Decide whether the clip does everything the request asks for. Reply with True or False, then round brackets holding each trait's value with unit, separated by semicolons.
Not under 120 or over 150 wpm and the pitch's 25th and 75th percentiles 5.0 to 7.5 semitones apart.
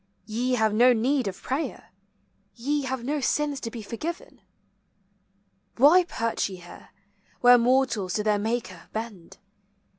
False (140 wpm; 3.8 semitones)